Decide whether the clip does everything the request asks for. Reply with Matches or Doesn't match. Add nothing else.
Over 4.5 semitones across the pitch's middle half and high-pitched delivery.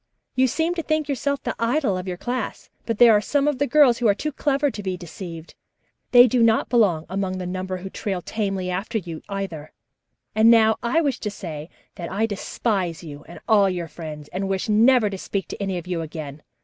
Matches